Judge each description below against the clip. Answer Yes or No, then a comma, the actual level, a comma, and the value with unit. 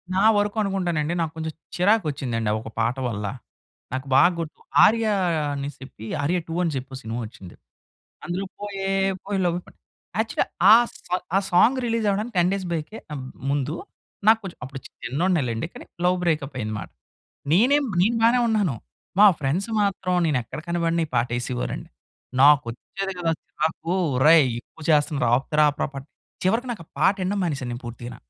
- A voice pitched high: No, medium, 165 Hz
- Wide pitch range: Yes, wide, 6.3 semitones